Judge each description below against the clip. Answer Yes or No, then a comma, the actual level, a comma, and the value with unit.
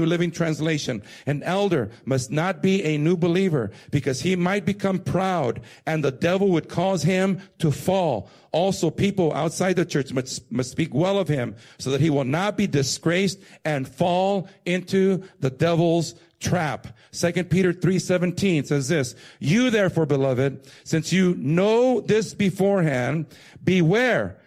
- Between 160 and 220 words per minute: No, average, 150 wpm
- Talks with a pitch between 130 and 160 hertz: No, medium, 170 Hz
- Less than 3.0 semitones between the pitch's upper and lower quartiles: No, average, 4.6 semitones